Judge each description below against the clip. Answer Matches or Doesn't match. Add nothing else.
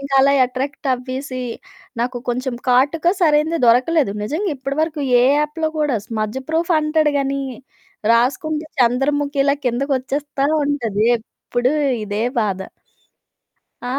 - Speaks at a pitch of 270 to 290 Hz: Matches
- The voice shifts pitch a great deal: Doesn't match